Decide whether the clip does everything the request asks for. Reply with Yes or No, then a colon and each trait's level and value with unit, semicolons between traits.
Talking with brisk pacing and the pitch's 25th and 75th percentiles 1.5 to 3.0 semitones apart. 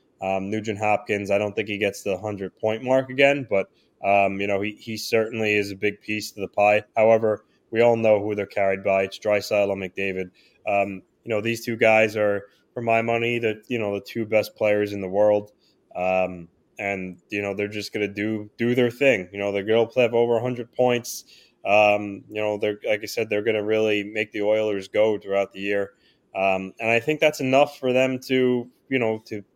Yes: fast, 225 wpm; narrow, 2.4 semitones